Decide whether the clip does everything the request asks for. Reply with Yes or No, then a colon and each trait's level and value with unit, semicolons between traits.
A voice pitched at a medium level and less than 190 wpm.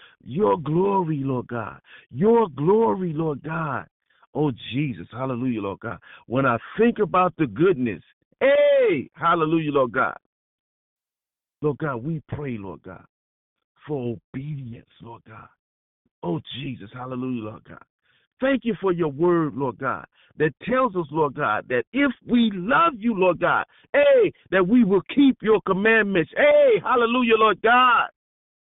Yes: medium, 165 Hz; average, 140 wpm